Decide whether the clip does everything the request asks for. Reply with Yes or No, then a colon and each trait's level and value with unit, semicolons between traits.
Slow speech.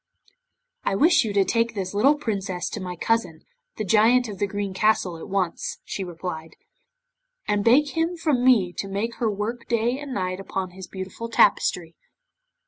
No: average, 175 wpm